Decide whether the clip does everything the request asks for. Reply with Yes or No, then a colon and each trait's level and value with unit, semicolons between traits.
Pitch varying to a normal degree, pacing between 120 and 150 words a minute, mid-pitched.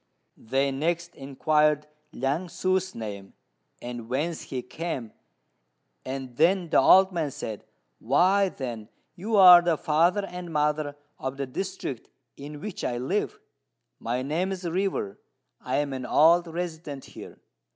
Yes: average, 4.9 semitones; average, 140 wpm; medium, 150 Hz